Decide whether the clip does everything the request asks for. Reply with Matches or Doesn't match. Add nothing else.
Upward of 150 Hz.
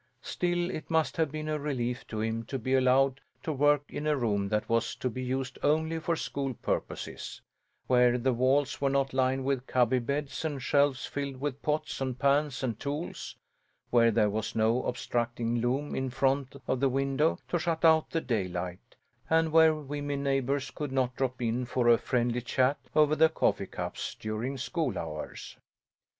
Doesn't match